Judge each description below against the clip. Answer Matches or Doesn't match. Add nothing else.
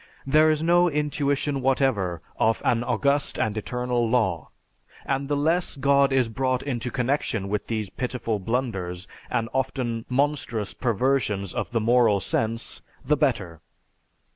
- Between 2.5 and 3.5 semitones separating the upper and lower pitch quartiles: Doesn't match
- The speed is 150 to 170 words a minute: Doesn't match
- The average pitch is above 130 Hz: Doesn't match